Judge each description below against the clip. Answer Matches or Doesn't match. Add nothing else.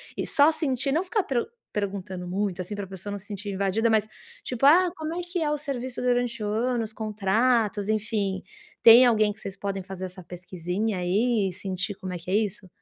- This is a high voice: Matches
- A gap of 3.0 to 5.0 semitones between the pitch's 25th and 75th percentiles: Matches